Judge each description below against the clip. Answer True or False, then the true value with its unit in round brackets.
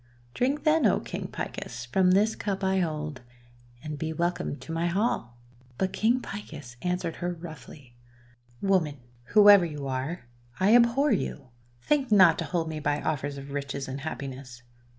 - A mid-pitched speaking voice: True (160 Hz)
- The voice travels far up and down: True (5.8 semitones)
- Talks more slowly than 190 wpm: True (170 wpm)